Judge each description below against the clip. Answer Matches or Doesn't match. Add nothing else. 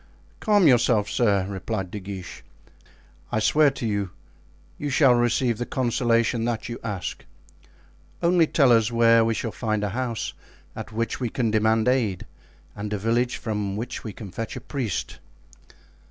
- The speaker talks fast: Doesn't match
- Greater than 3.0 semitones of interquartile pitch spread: Doesn't match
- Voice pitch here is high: Doesn't match